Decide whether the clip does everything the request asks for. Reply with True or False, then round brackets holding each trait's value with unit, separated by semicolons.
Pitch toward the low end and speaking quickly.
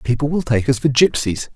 True (130 Hz; 230 wpm)